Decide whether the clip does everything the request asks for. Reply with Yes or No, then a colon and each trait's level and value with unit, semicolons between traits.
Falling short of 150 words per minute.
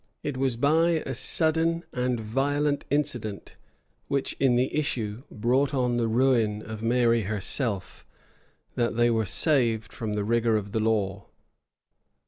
Yes: average, 140 wpm